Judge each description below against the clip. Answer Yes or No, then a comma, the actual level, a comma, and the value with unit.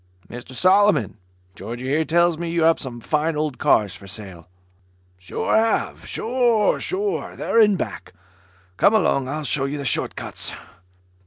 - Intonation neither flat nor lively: No, wide, 8.6 semitones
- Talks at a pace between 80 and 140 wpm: No, average, 155 wpm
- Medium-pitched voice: Yes, medium, 155 Hz